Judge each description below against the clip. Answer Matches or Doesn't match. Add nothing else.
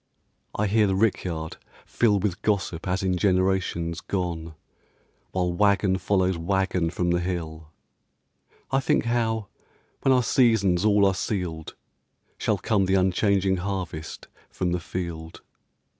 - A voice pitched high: Doesn't match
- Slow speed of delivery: Matches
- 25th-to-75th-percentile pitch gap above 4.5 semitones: Doesn't match